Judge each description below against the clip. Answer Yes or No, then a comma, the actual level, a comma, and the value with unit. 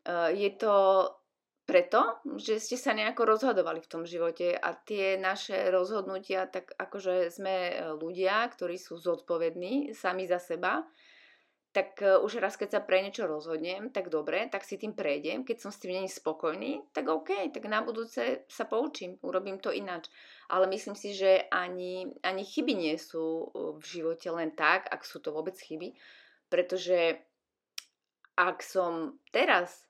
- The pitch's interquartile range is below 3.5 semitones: No, average, 3.8 semitones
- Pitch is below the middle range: No, high, 190 Hz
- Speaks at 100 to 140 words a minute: No, average, 155 wpm